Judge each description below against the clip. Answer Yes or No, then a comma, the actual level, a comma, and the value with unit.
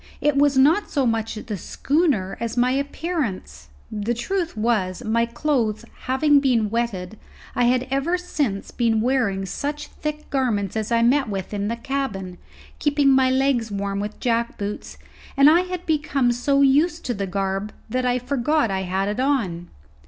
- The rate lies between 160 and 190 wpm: Yes, average, 165 wpm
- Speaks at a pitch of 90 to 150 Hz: No, high, 240 Hz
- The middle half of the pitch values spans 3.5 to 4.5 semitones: No, average, 5.1 semitones